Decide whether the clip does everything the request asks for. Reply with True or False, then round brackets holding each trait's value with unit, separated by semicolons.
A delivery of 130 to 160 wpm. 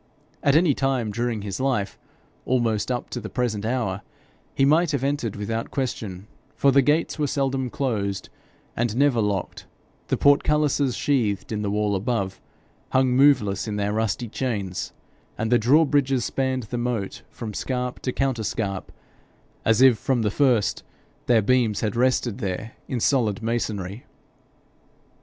True (150 wpm)